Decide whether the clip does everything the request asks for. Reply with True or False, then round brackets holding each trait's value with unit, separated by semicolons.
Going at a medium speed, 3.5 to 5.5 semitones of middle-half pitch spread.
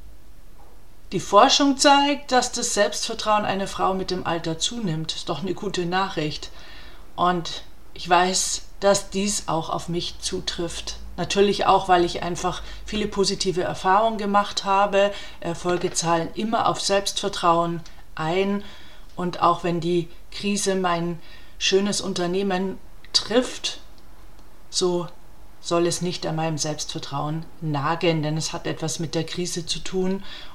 False (135 wpm; 2.9 semitones)